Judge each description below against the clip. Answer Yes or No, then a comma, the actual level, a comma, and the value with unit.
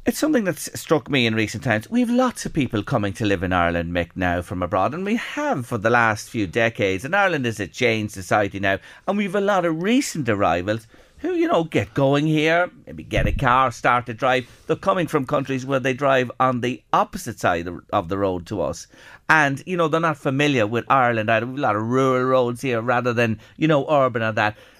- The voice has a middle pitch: No, low, 125 Hz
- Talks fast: Yes, fast, 225 wpm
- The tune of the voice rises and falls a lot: Yes, wide, 6.5 semitones